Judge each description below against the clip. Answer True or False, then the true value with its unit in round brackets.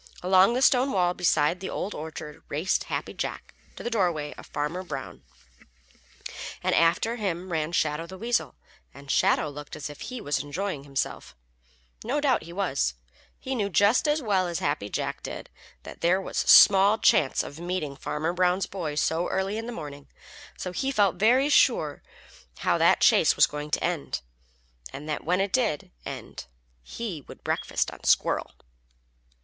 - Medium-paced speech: True (170 wpm)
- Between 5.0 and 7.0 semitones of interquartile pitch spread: True (5.4 semitones)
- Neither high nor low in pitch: True (180 Hz)